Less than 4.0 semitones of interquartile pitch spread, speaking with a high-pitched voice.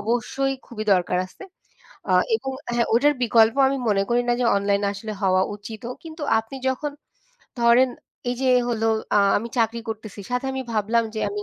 Yes: average, 2.9 semitones; high, 230 Hz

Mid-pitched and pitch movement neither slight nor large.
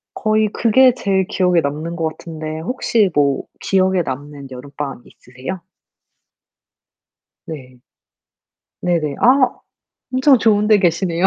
No: medium, 170 Hz; wide, 6.1 semitones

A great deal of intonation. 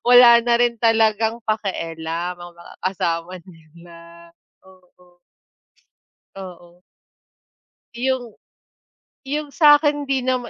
Yes: wide, 6.0 semitones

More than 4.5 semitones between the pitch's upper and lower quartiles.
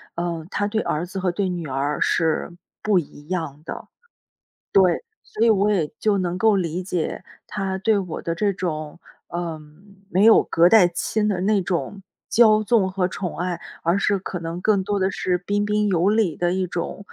No: average, 3.0 semitones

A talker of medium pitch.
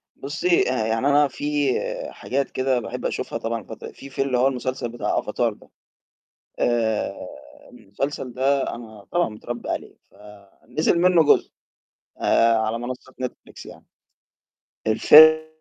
No: low, 130 Hz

